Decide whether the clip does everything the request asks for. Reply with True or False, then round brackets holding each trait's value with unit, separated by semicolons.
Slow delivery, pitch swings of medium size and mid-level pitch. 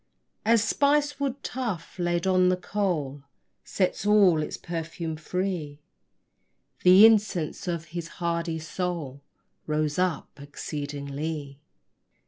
True (110 wpm; 3.8 semitones; 170 Hz)